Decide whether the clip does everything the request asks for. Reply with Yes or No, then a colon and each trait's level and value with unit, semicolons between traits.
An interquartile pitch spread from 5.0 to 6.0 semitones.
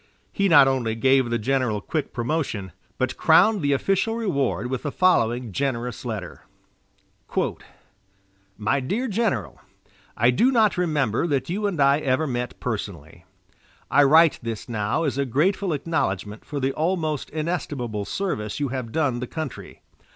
Yes: wide, 5.6 semitones